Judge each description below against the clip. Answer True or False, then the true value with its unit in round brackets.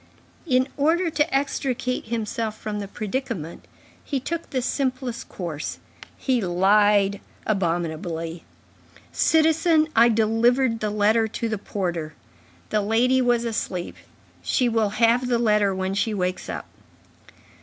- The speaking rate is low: True (125 wpm)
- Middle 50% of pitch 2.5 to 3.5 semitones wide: False (4.3 semitones)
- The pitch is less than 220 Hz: False (225 Hz)